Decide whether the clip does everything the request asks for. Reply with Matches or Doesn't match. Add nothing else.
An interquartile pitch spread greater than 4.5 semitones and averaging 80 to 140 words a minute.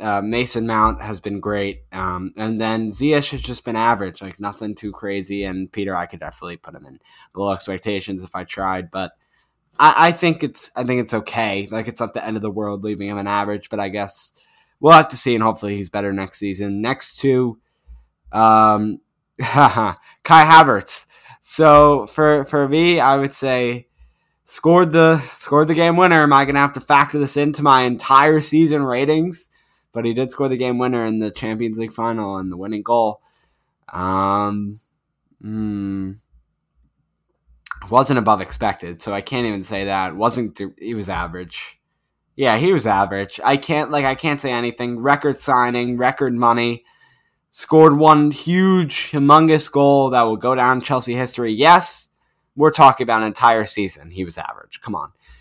Doesn't match